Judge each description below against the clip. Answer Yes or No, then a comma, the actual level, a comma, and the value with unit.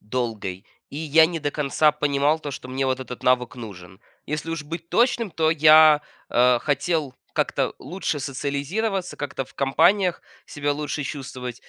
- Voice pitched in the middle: Yes, medium, 145 Hz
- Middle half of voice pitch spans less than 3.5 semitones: No, average, 3.8 semitones